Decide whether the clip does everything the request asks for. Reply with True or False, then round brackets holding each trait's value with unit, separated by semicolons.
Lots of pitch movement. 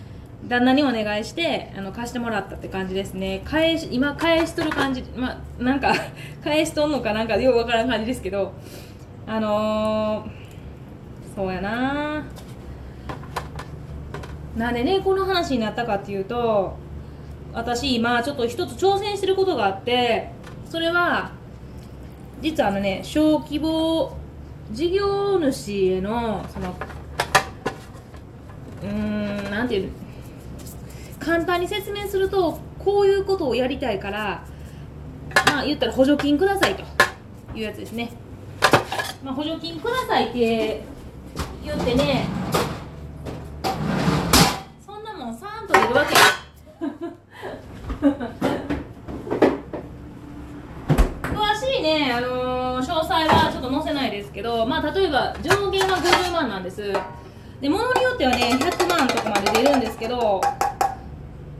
True (7.7 semitones)